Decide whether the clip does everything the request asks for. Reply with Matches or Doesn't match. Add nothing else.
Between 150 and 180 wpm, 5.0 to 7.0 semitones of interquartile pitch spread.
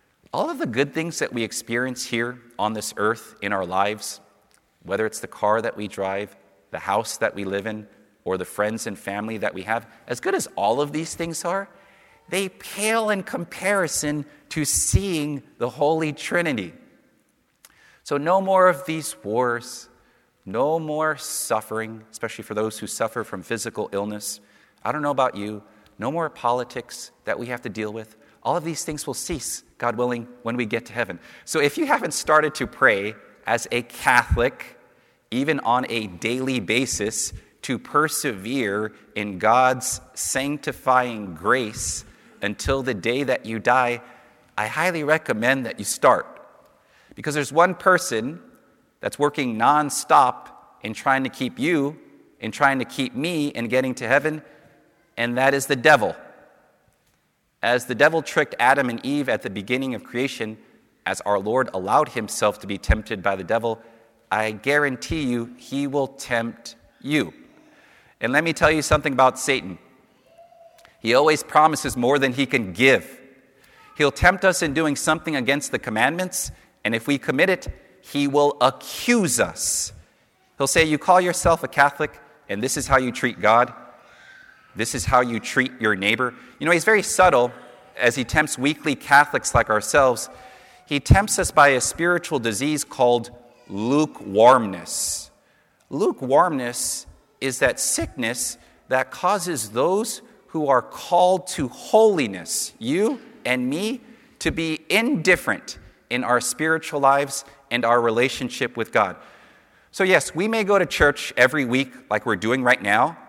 Matches